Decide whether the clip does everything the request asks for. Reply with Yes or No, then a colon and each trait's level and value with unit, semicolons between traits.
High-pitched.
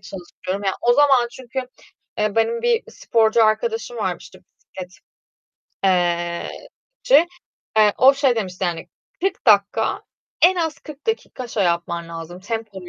Yes: high, 220 Hz